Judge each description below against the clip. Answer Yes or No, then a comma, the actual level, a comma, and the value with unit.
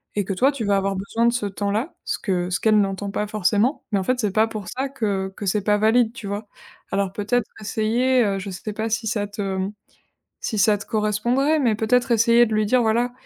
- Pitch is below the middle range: No, high, 215 Hz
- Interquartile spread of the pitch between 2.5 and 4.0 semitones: Yes, average, 2.8 semitones